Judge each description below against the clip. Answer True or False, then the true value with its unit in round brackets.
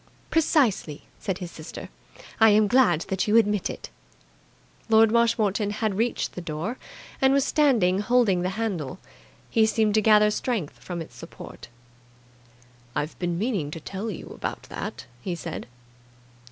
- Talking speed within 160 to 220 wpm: False (150 wpm)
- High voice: True (210 Hz)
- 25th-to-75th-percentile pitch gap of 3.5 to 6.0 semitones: True (4.1 semitones)